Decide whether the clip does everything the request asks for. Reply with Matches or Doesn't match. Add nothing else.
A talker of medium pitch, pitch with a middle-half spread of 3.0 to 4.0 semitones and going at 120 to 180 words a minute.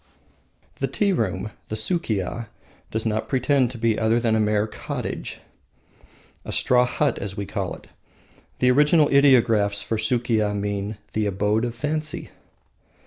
Doesn't match